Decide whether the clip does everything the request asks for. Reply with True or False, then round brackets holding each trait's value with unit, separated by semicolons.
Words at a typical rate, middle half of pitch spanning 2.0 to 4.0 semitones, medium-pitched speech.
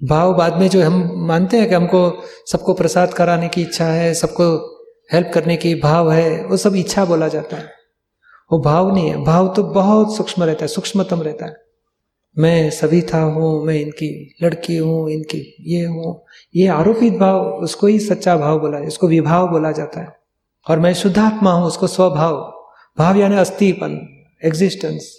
True (175 wpm; 2.7 semitones; 170 Hz)